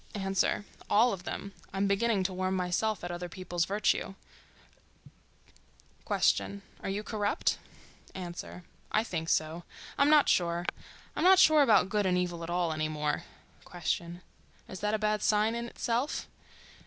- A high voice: Yes, high, 195 Hz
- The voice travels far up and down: No, average, 3.5 semitones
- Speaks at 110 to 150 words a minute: Yes, average, 140 wpm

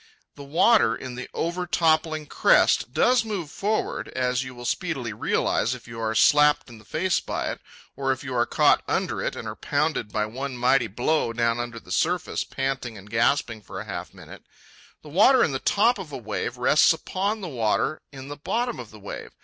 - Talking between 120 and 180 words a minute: No, fast, 205 wpm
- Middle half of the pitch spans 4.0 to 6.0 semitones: Yes, wide, 5.6 semitones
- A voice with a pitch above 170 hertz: No, low, 135 Hz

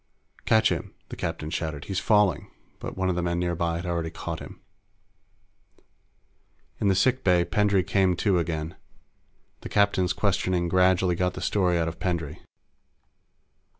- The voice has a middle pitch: No, very low, 90 Hz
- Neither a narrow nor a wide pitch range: No, narrow, 2.1 semitones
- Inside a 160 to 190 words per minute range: No, average, 150 wpm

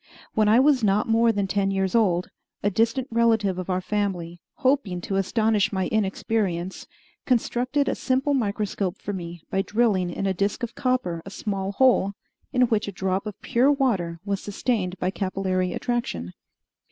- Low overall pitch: No, high, 200 Hz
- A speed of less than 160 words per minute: No, average, 170 wpm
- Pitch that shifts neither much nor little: Yes, average, 3.8 semitones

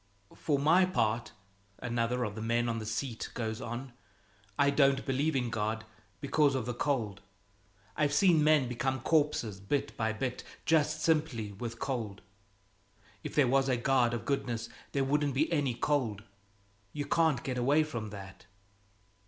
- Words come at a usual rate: Yes, average, 160 wpm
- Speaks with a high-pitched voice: No, low, 130 Hz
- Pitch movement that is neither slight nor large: Yes, average, 4.1 semitones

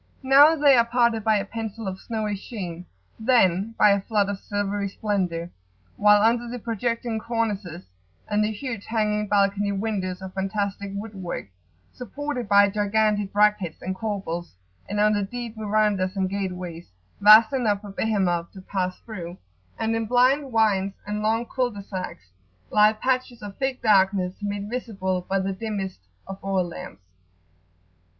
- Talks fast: No, average, 155 wpm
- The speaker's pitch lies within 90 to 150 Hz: No, high, 205 Hz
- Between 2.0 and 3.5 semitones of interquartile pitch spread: Yes, narrow, 2.6 semitones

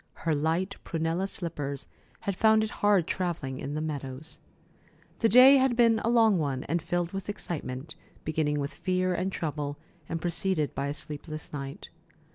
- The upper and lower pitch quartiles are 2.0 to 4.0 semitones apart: No, average, 4.7 semitones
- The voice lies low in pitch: No, medium, 165 Hz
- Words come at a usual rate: Yes, average, 165 wpm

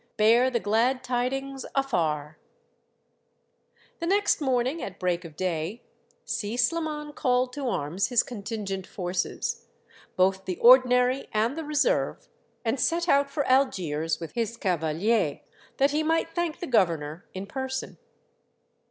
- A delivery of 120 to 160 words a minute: Yes, average, 140 wpm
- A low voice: No, high, 240 Hz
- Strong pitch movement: Yes, wide, 6.6 semitones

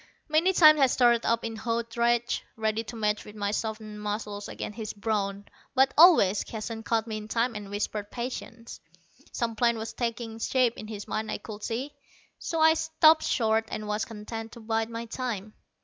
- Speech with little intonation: Yes, narrow, 1.9 semitones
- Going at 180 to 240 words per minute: Yes, average, 185 wpm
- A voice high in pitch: Yes, high, 225 Hz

